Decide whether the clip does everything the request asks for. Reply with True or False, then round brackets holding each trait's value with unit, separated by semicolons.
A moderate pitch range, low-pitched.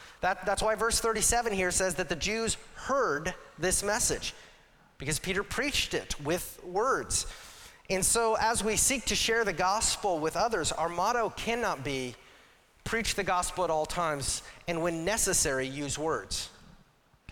False (4.5 semitones; 190 Hz)